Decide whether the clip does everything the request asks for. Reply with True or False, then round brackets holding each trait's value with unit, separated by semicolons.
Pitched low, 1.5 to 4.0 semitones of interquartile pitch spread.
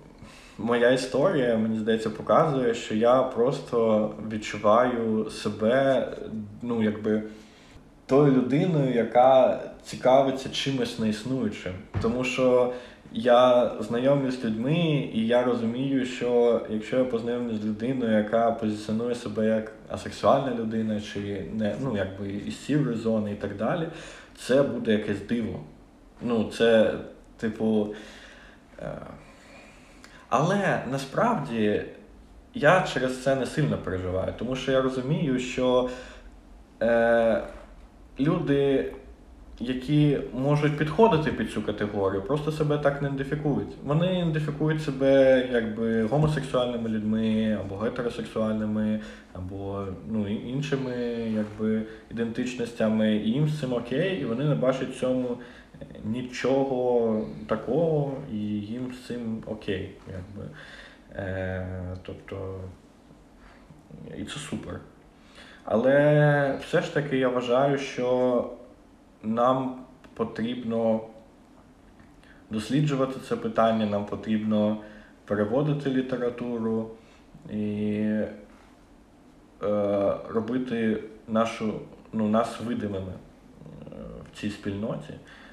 True (115 Hz; 3.4 semitones)